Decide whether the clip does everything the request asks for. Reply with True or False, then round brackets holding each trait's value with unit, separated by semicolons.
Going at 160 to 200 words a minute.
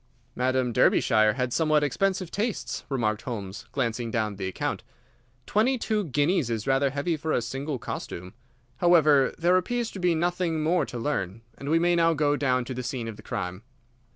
True (180 wpm)